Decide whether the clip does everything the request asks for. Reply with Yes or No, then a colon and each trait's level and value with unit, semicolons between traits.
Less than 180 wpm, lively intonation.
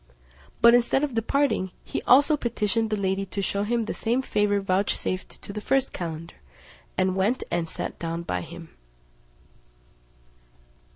No: average, 150 wpm; average, 4.2 semitones